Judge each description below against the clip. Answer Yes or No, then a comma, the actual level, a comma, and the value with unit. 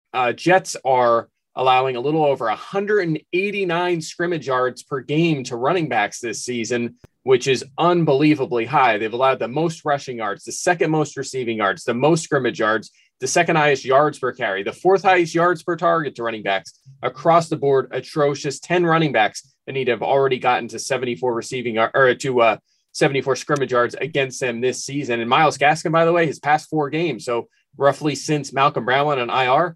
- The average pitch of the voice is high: No, medium, 140 Hz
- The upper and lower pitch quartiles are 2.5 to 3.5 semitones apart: No, average, 4.7 semitones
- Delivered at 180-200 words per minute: Yes, average, 190 wpm